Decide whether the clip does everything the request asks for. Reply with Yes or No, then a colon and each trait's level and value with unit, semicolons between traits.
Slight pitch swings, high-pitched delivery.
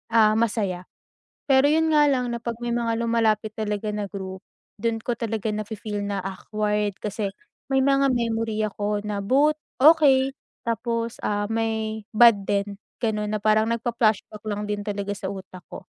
Yes: narrow, 2.3 semitones; high, 215 Hz